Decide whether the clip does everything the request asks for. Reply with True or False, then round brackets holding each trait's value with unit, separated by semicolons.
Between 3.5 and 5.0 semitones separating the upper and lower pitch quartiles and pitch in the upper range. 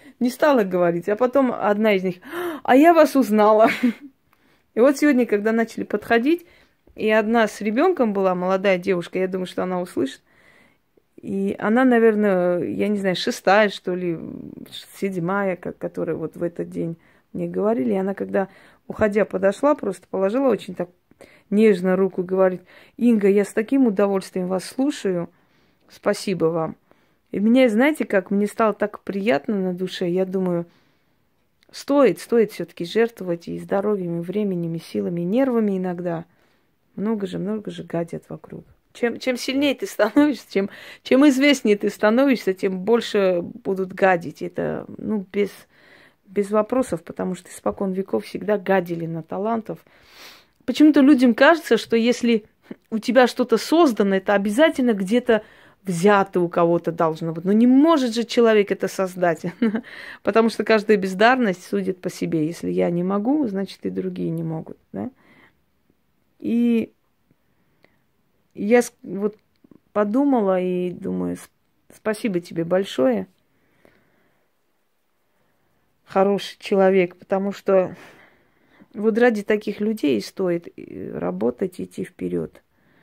True (4.2 semitones; 205 Hz)